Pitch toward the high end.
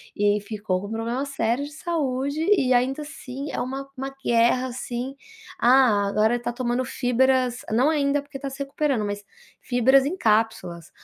Yes: very high, 255 Hz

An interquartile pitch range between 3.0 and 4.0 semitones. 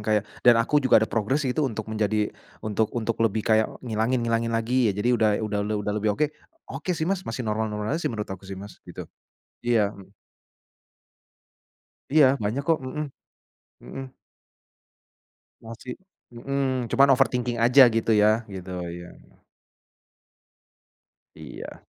Yes: average, 3.3 semitones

